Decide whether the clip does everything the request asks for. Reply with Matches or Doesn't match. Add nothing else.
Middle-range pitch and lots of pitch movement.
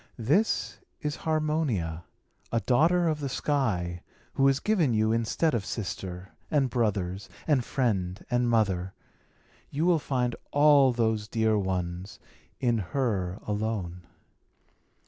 Doesn't match